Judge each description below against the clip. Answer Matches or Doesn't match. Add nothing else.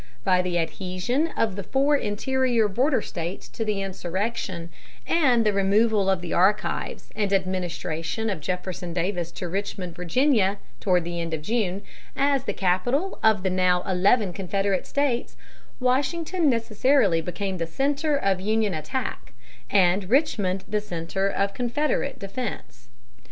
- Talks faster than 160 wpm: Doesn't match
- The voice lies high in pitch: Matches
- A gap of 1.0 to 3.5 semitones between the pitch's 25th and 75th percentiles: Doesn't match